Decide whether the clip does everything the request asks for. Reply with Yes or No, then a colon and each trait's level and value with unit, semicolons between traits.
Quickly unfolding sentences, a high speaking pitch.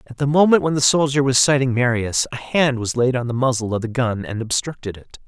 No: fast, 250 wpm; low, 125 Hz